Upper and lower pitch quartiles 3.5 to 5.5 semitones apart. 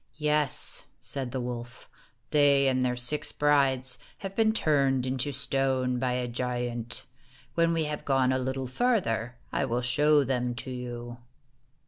No: average, 2.9 semitones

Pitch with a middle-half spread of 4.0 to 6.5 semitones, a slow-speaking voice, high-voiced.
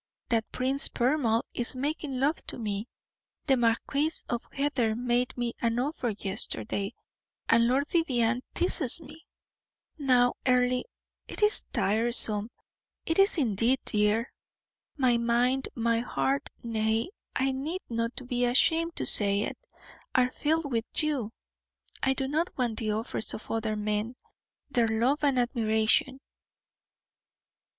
No: average, 3.3 semitones; slow, 130 wpm; high, 245 Hz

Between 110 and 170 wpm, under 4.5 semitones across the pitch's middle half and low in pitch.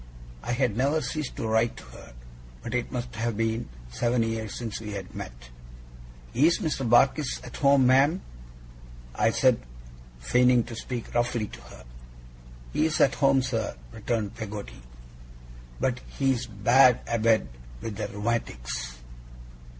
Yes: average, 140 wpm; average, 2.9 semitones; low, 120 Hz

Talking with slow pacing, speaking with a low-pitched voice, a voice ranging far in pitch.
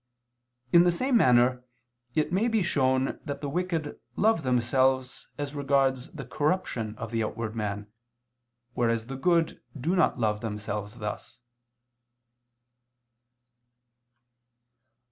Yes: slow, 115 wpm; low, 130 Hz; wide, 6.0 semitones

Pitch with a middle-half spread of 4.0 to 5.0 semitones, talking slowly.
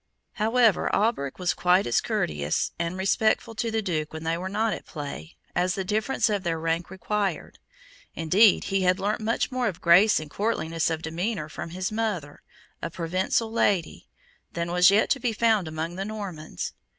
No: average, 4.7 semitones; average, 180 wpm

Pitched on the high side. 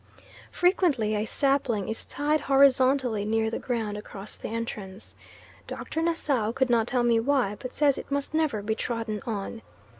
Yes: high, 235 Hz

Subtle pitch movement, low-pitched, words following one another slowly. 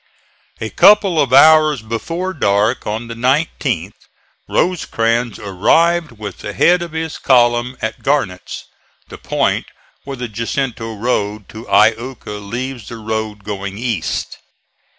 No: average, 4.8 semitones; low, 115 Hz; slow, 130 wpm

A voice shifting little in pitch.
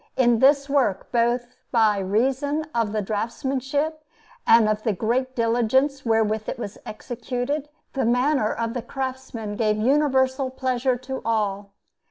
No: average, 3.3 semitones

